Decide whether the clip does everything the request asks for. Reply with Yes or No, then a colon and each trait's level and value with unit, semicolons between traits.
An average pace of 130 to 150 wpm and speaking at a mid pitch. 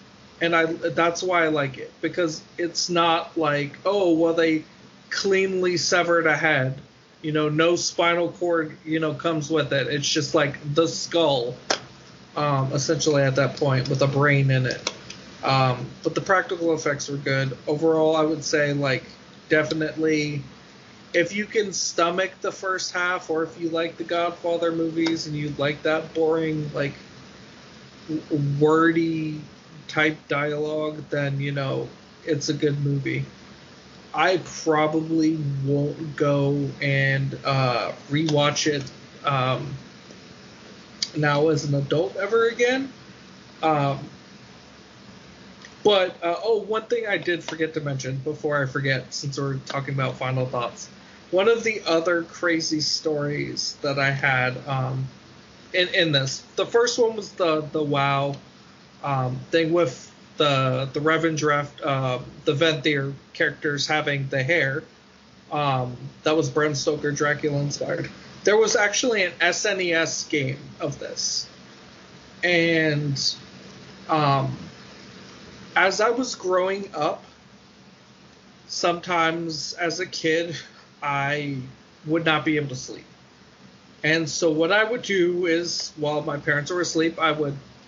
Yes: average, 140 wpm; medium, 155 Hz